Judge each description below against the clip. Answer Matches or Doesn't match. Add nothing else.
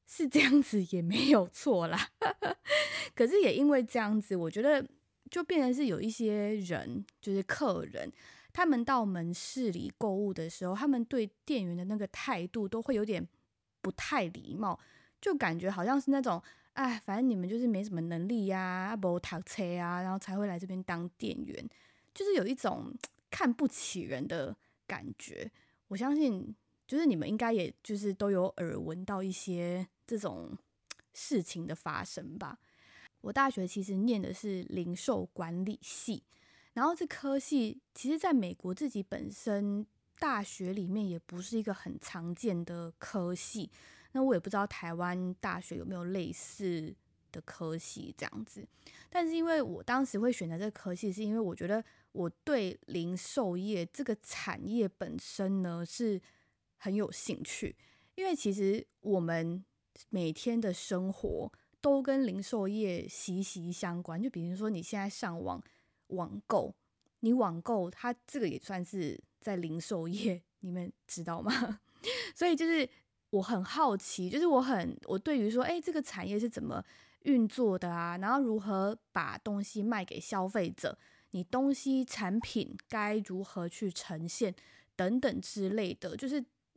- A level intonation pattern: Doesn't match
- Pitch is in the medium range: Doesn't match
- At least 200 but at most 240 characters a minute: Matches